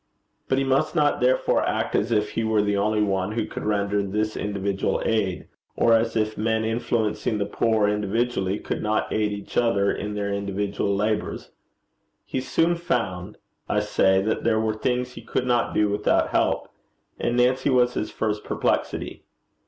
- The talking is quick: No, average, 175 wpm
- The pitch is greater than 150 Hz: No, low, 110 Hz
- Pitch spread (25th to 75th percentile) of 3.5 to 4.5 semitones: No, narrow, 2.5 semitones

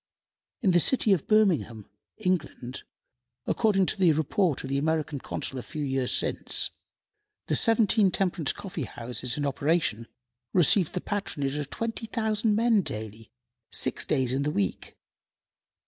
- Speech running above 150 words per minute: No, average, 140 wpm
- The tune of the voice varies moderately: No, wide, 7.3 semitones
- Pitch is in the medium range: Yes, medium, 160 Hz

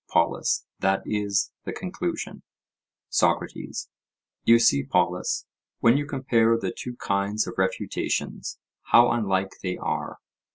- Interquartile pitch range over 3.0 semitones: Yes, average, 3.4 semitones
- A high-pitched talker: No, low, 105 Hz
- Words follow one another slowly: Yes, slow, 120 wpm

